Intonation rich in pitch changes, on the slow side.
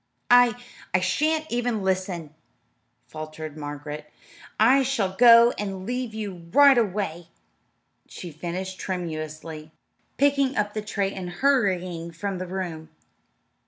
Yes: wide, 5.9 semitones; slow, 120 wpm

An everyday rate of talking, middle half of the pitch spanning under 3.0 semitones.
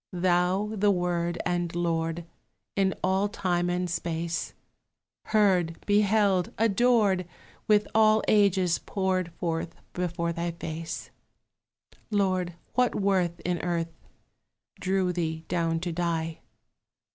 No: slow, 110 wpm; narrow, 2.6 semitones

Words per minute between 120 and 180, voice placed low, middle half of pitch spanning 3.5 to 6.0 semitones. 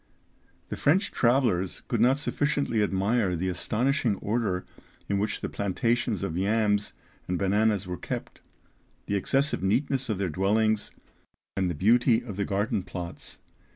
Yes: average, 145 wpm; low, 105 Hz; average, 4.0 semitones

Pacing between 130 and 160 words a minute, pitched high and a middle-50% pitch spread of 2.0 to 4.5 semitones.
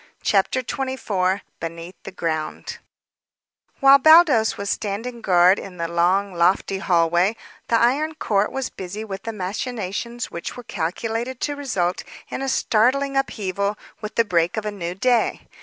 No: average, 150 wpm; high, 205 Hz; average, 5.2 semitones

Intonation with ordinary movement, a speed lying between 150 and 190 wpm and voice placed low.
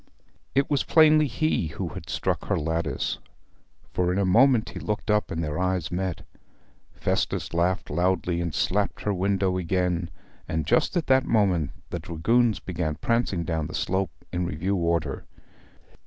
Yes: average, 4.0 semitones; average, 160 wpm; very low, 90 Hz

